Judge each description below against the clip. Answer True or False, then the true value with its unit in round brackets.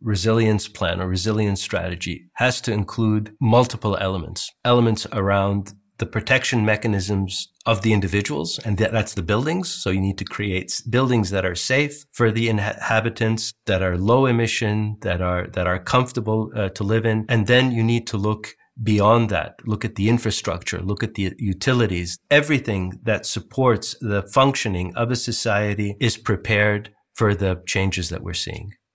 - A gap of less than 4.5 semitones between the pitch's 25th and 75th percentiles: True (2.9 semitones)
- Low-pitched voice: True (110 Hz)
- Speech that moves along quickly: False (165 wpm)